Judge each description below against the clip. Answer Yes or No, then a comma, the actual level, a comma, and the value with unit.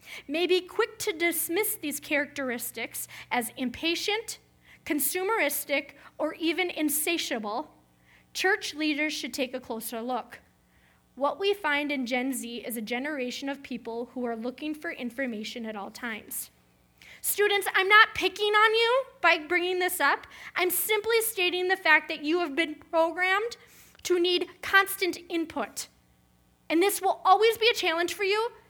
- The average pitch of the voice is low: No, very high, 325 Hz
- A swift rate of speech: No, average, 150 wpm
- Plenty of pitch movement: Yes, wide, 6.5 semitones